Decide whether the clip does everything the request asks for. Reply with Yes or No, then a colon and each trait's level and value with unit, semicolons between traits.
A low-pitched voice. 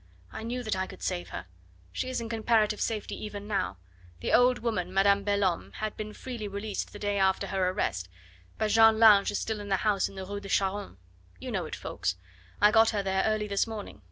No: high, 205 Hz